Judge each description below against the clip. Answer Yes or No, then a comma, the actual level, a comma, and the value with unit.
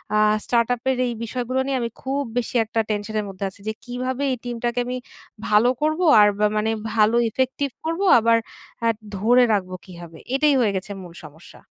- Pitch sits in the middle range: No, high, 235 Hz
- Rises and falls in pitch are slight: No, average, 3.5 semitones